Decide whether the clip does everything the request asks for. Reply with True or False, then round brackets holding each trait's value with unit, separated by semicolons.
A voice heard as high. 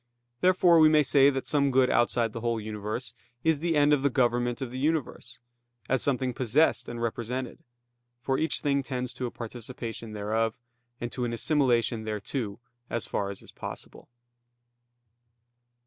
False (125 Hz)